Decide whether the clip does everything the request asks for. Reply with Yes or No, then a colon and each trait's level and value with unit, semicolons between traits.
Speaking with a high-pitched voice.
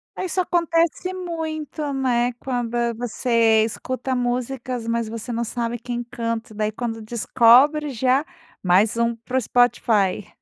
Yes: high, 240 Hz